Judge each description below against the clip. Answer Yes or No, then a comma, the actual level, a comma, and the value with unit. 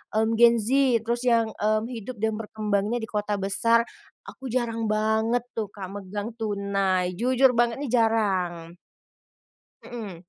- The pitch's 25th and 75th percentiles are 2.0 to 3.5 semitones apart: Yes, narrow, 2.5 semitones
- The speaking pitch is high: Yes, high, 220 Hz